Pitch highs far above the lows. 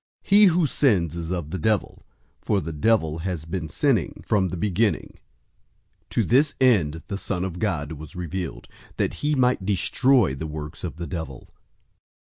Yes: wide, 5.7 semitones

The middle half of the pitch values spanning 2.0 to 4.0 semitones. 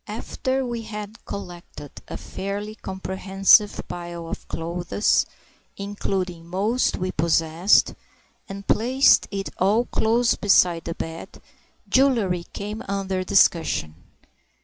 Yes: average, 3.4 semitones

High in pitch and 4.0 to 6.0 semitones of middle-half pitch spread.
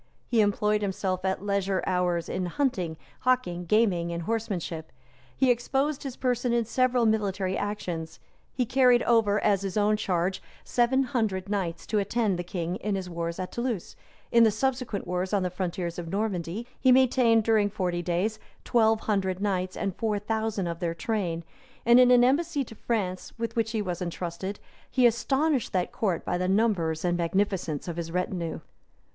Yes: high, 200 Hz; average, 4.4 semitones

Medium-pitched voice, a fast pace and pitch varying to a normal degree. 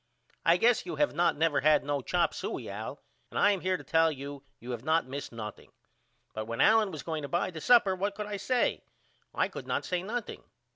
No: medium, 165 Hz; fast, 230 wpm; wide, 6.0 semitones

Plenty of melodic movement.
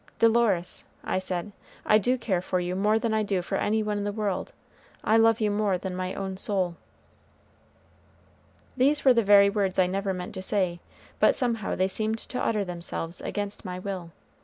No: average, 2.8 semitones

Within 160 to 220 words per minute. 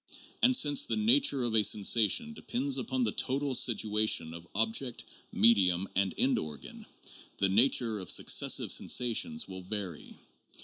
No: average, 140 wpm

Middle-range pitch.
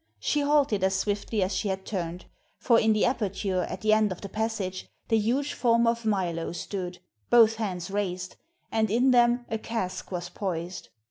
No: high, 210 Hz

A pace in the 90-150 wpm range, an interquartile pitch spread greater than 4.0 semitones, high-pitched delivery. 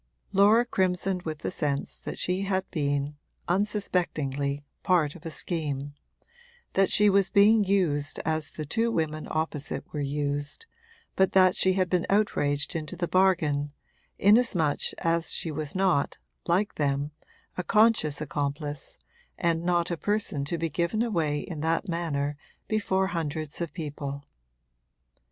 No: average, 140 wpm; average, 4.4 semitones; medium, 165 Hz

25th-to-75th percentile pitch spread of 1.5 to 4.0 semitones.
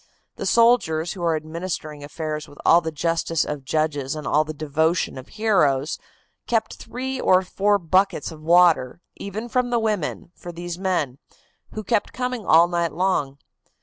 No: average, 4.5 semitones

